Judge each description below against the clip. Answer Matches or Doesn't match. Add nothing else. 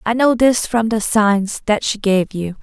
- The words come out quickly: Matches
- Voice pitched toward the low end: Doesn't match